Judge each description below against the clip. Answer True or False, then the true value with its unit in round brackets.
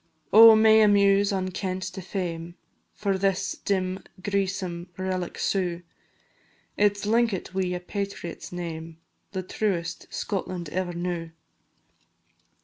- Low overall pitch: False (185 Hz)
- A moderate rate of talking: False (120 wpm)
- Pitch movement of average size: False (2.1 semitones)